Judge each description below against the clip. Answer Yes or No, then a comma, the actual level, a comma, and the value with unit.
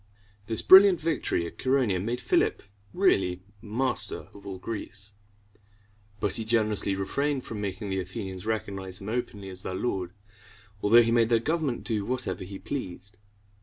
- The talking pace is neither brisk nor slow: Yes, average, 155 wpm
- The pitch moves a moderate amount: Yes, average, 4.0 semitones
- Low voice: Yes, low, 105 Hz